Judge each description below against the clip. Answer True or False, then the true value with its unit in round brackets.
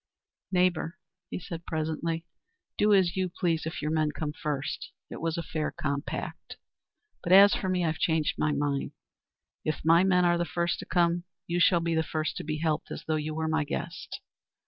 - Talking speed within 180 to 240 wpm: True (195 wpm)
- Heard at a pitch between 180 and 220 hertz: False (165 Hz)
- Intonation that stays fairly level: True (1.9 semitones)